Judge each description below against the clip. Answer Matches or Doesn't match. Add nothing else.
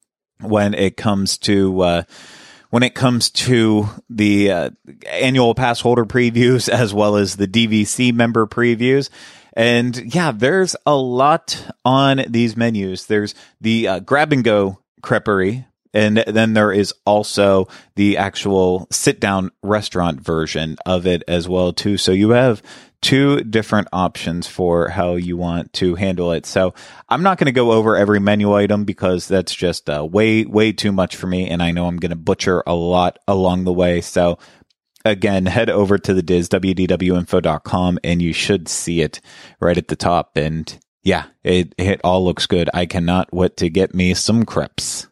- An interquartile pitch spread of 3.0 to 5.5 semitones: Matches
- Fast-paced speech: Doesn't match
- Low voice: Matches